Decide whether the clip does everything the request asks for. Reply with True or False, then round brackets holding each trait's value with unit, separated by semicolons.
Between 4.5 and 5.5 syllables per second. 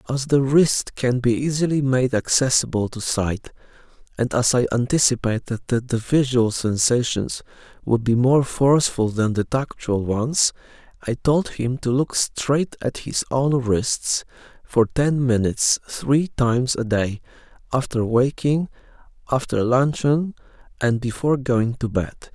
False (4.1 syllables/s)